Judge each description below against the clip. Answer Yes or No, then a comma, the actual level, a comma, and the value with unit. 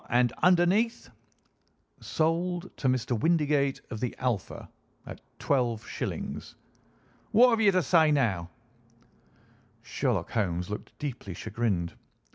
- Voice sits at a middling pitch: No, low, 130 Hz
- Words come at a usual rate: No, slow, 105 wpm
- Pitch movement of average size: No, wide, 7.6 semitones